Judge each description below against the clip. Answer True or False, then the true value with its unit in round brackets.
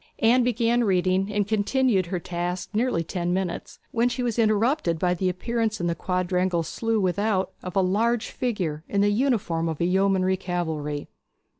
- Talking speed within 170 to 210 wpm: True (175 wpm)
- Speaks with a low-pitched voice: False (190 Hz)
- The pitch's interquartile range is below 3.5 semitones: False (4.2 semitones)